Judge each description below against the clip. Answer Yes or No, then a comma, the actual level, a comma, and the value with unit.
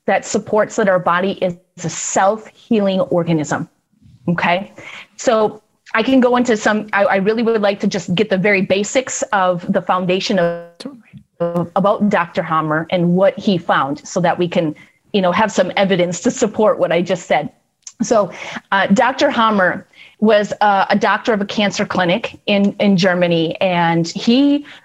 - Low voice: No, high, 195 Hz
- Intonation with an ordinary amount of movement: Yes, average, 3.4 semitones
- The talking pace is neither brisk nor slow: Yes, average, 170 wpm